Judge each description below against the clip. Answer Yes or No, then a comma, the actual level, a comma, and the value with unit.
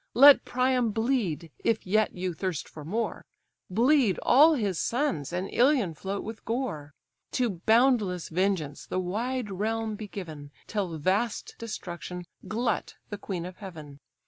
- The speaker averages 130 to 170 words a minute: Yes, average, 145 wpm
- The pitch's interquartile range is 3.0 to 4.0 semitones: No, average, 4.9 semitones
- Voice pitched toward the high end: Yes, high, 205 Hz